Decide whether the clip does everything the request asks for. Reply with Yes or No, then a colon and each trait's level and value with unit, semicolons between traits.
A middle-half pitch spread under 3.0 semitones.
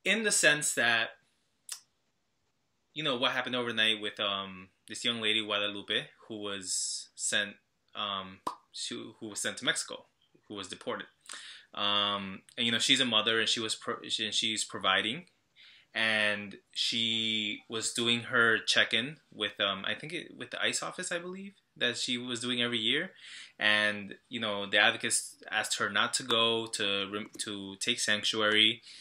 Yes: narrow, 2.6 semitones